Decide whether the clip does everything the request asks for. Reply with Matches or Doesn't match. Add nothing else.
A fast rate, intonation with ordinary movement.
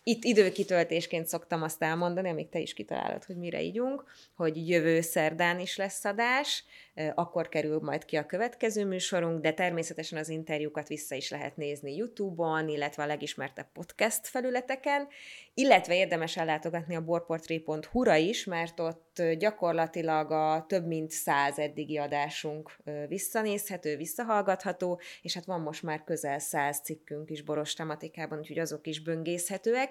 Doesn't match